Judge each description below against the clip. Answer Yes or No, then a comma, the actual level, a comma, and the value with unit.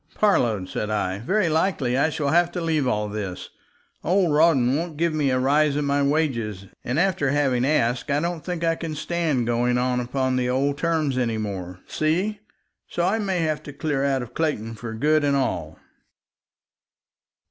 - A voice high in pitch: No, medium, 140 Hz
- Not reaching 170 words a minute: No, average, 180 wpm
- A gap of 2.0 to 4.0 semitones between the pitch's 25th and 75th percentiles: No, average, 4.8 semitones